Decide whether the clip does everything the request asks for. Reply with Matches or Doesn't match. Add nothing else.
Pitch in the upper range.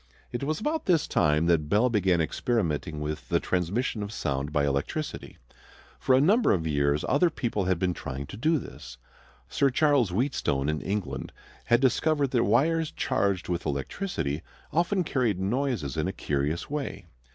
Doesn't match